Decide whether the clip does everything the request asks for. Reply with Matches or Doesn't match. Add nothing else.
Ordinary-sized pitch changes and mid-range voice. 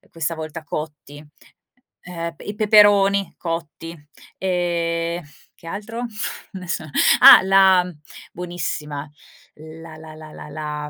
Matches